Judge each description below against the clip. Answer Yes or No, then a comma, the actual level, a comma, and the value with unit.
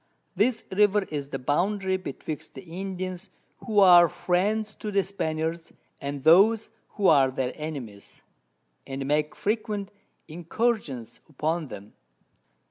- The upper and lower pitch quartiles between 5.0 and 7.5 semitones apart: Yes, wide, 5.6 semitones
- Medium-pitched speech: Yes, medium, 175 Hz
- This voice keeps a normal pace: No, slow, 125 wpm